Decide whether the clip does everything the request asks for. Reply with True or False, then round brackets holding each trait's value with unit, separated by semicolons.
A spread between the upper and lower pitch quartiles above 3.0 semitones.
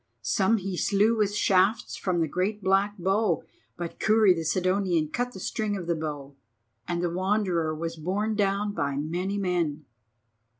True (3.5 semitones)